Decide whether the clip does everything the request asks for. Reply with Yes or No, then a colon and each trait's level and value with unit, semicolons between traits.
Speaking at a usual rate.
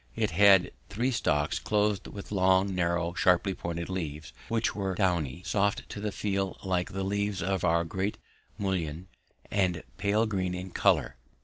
Yes: average, 155 wpm